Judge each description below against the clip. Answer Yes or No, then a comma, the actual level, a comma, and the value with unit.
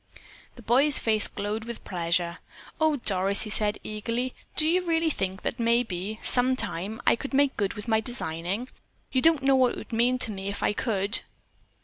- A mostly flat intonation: No, average, 4.3 semitones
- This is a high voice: Yes, high, 230 Hz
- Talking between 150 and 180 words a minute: No, average, 190 wpm